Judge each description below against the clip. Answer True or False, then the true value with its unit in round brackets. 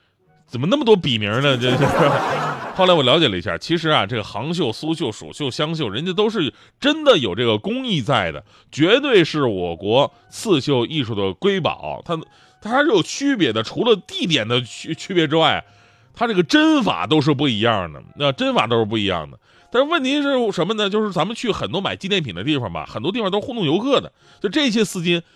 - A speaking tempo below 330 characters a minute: True (310 characters per minute)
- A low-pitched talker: False (160 Hz)